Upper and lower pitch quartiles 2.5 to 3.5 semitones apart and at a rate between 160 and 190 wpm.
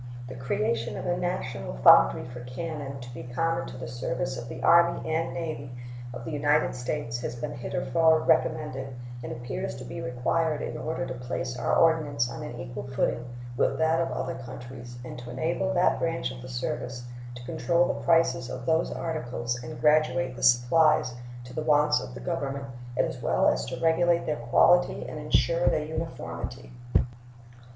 No: average, 4.6 semitones; average, 180 wpm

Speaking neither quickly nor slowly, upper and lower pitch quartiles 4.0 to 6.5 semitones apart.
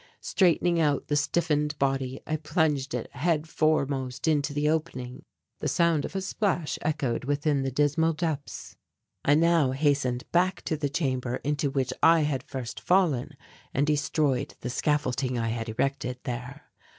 No: average, 155 wpm; average, 3.1 semitones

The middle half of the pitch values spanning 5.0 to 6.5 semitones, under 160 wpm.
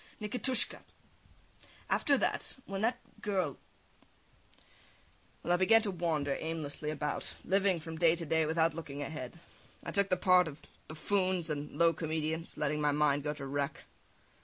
No: average, 3.7 semitones; average, 150 wpm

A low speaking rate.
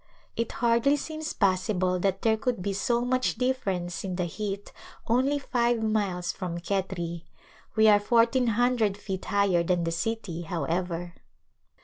No: average, 150 wpm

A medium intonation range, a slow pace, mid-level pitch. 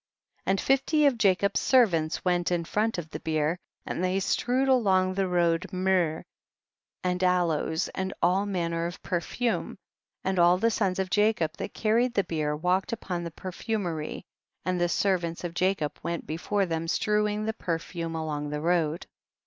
No: average, 3.2 semitones; average, 165 wpm; medium, 180 Hz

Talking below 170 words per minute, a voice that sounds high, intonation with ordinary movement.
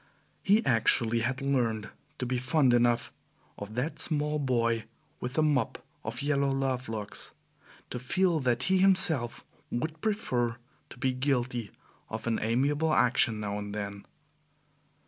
No: average, 145 wpm; low, 125 Hz; average, 4.0 semitones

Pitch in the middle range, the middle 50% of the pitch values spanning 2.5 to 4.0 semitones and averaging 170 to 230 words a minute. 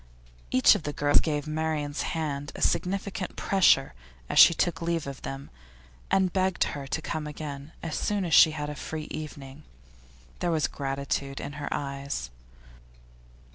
No: medium, 150 Hz; average, 2.8 semitones; average, 160 wpm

